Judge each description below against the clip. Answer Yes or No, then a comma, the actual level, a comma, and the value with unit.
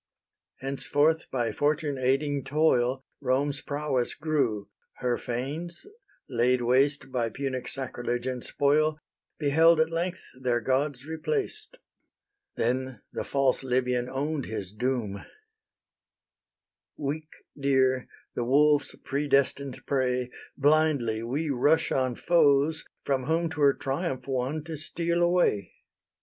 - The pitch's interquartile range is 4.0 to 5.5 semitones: No, average, 3.3 semitones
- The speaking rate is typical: No, slow, 110 wpm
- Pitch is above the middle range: No, medium, 140 Hz